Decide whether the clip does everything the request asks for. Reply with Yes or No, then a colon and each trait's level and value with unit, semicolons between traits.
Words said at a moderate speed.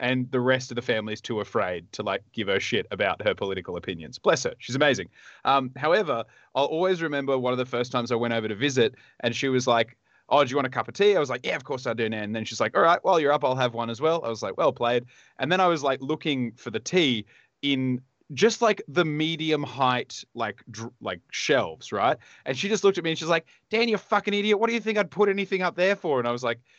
No: fast, 275 wpm